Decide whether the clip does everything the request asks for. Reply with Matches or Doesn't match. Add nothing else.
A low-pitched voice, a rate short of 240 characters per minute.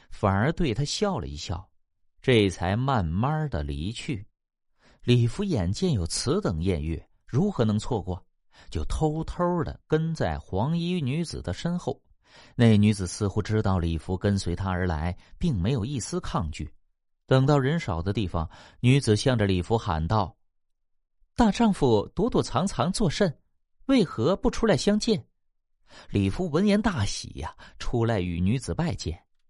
Matches